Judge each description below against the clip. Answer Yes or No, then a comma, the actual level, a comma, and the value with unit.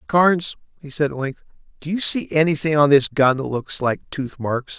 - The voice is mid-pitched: Yes, medium, 150 Hz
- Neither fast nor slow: No, fast, 215 wpm